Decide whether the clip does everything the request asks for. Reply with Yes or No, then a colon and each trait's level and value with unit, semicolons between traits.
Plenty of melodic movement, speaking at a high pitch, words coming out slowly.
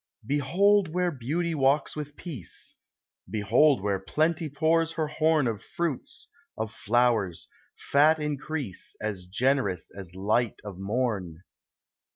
No: wide, 7.3 semitones; low, 135 Hz; slow, 120 wpm